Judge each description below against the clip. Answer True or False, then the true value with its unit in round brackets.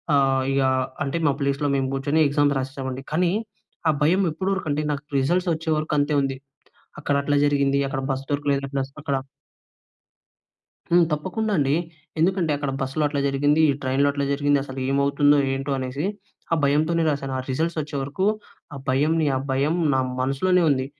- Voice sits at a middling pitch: True (145 Hz)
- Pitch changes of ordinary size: False (2.2 semitones)